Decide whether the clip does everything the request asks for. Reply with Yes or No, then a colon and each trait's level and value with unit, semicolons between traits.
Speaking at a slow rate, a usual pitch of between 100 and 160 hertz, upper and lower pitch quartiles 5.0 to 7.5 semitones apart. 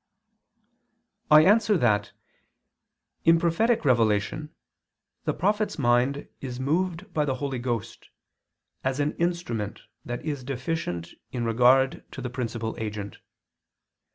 Yes: slow, 115 wpm; low, 135 Hz; wide, 5.5 semitones